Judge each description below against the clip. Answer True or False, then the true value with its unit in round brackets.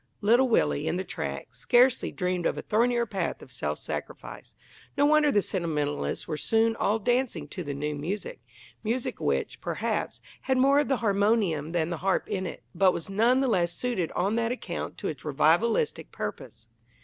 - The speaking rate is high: False (185 wpm)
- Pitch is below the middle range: False (205 Hz)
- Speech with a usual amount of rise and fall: False (6.0 semitones)